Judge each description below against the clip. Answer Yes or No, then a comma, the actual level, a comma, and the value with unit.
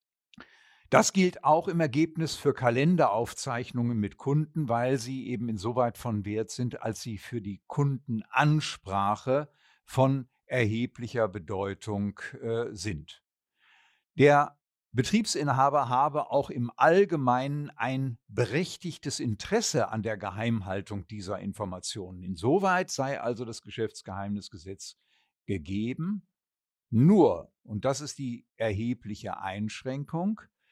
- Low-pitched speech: Yes, low, 120 Hz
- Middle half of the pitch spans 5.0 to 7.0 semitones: Yes, wide, 5.4 semitones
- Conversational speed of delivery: No, slow, 105 wpm